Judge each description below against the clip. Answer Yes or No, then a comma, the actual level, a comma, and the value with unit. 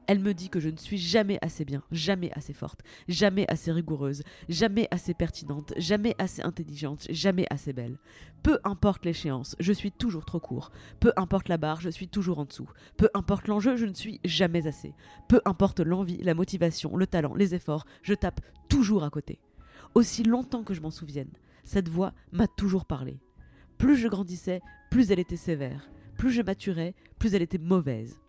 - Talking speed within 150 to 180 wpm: No, average, 190 wpm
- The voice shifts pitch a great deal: No, average, 4.3 semitones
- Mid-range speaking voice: Yes, medium, 180 Hz